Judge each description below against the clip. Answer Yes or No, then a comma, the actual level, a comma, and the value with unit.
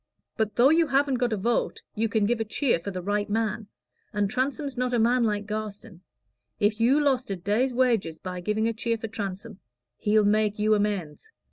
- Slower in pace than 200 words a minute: No, fast, 205 wpm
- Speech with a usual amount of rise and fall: Yes, average, 3.0 semitones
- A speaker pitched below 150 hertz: No, high, 220 Hz